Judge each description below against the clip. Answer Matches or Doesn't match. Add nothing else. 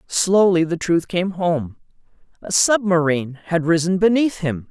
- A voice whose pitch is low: Doesn't match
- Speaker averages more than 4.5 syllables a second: Doesn't match